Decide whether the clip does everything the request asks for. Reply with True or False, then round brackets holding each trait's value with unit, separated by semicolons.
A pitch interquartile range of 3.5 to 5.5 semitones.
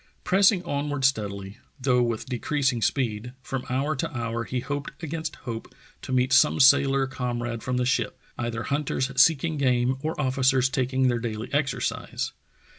False (2.6 semitones)